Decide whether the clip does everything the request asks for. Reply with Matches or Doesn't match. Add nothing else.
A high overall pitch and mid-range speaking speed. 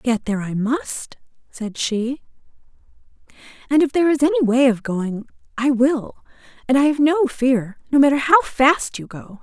Matches